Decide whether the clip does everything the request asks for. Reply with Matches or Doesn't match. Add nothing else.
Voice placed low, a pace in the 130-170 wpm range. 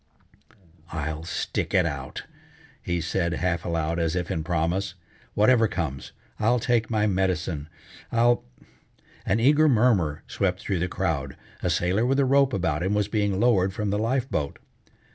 Matches